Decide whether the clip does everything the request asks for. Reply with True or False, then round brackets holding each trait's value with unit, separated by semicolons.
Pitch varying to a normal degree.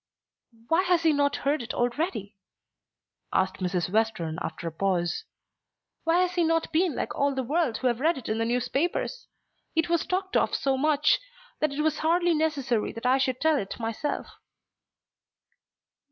False (6.2 semitones)